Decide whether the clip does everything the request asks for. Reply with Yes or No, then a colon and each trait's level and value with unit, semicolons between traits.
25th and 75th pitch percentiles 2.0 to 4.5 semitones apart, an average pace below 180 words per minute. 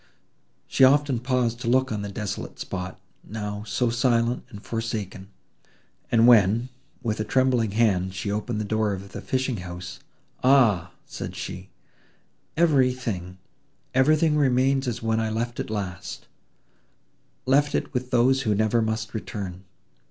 Yes: average, 3.9 semitones; slow, 135 wpm